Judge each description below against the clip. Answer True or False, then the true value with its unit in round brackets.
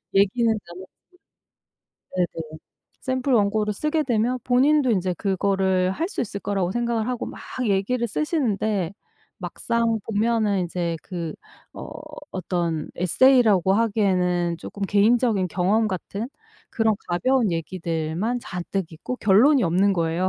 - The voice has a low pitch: False (200 Hz)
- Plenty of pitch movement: False (4.5 semitones)